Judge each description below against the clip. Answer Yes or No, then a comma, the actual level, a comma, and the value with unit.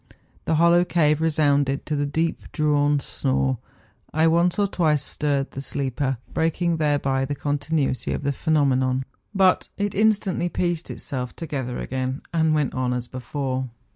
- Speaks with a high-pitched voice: No, medium, 145 Hz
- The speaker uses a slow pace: No, average, 150 wpm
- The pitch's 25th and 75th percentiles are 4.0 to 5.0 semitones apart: No, average, 3.5 semitones